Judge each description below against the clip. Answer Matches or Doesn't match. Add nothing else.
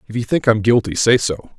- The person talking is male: Matches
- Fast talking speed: Matches